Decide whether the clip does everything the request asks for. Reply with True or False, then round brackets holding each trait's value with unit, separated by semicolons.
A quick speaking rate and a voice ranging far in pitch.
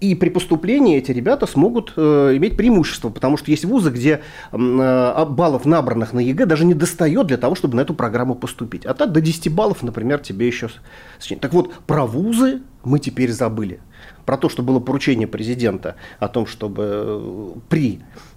True (180 wpm; 5.7 semitones)